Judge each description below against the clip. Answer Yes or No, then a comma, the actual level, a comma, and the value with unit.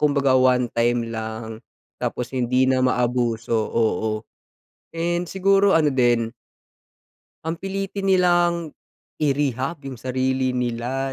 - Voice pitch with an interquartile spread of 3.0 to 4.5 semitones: No, average, 5.3 semitones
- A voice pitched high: No, low, 130 Hz